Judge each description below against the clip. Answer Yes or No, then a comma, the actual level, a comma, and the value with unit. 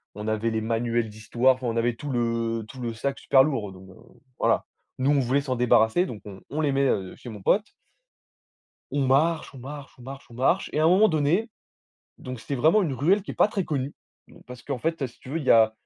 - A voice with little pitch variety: No, average, 4.1 semitones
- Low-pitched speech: Yes, low, 130 Hz